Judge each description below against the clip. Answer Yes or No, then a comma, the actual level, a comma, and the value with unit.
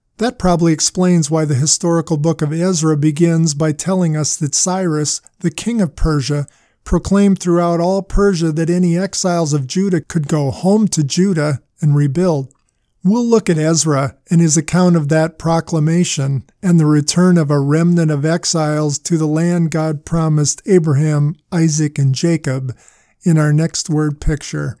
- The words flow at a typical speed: Yes, average, 160 wpm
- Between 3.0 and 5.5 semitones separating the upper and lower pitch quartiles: No, narrow, 2.6 semitones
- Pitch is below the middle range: No, medium, 160 Hz